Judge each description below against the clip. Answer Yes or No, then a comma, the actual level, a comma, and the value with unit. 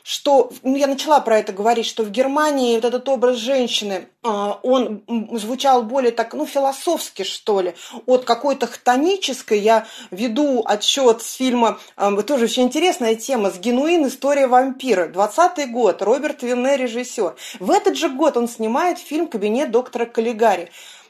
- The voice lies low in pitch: No, very high, 250 Hz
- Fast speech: No, average, 150 wpm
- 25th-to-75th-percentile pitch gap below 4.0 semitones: Yes, average, 3.6 semitones